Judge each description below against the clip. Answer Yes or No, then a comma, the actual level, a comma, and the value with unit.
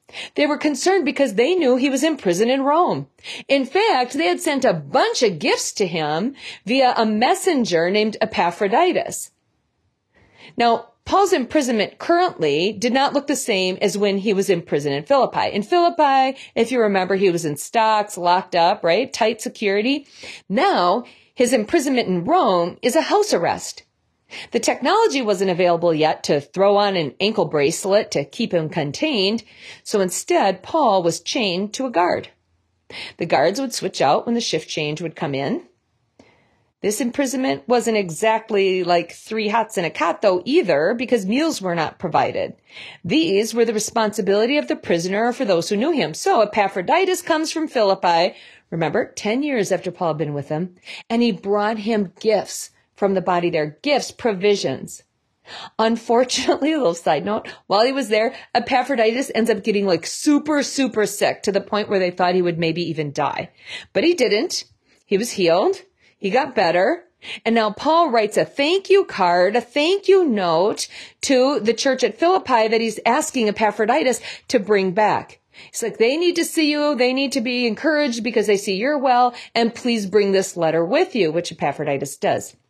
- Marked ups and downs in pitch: Yes, wide, 6.5 semitones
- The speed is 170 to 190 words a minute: Yes, average, 180 wpm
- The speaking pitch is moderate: No, high, 225 Hz